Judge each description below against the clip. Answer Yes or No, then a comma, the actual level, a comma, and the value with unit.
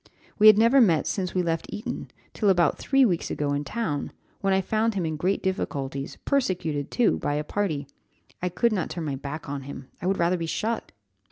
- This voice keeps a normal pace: No, fast, 210 wpm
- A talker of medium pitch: Yes, medium, 180 Hz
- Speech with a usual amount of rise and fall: No, wide, 5.8 semitones